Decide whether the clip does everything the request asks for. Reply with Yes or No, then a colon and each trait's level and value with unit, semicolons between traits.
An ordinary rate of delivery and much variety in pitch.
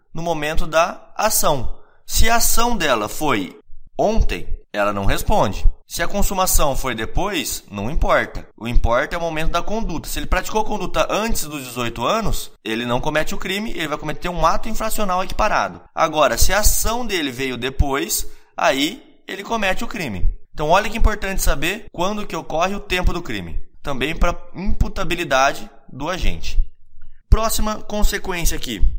Yes: average, 165 wpm; wide, 8.3 semitones